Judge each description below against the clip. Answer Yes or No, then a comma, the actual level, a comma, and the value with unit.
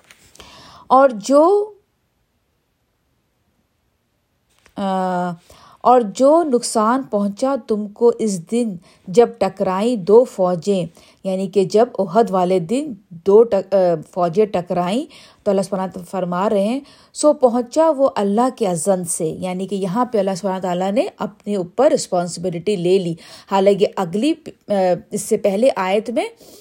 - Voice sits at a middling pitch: No, high, 205 Hz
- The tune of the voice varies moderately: Yes, average, 4.3 semitones